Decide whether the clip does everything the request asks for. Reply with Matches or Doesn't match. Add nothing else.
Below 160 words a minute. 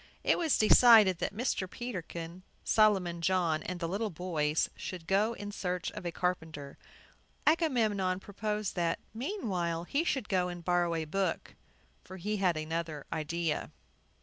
Matches